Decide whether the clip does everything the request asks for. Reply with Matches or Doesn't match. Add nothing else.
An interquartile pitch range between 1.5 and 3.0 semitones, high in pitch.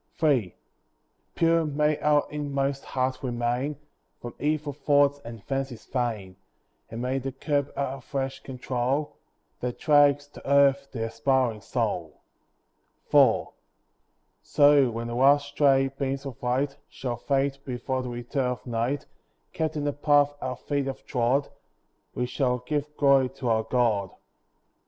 Doesn't match